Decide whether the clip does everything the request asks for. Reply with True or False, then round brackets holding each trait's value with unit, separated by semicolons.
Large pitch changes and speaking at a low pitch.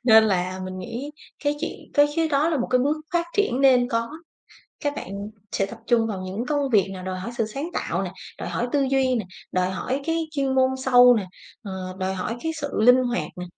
False (5.8 semitones; 245 Hz)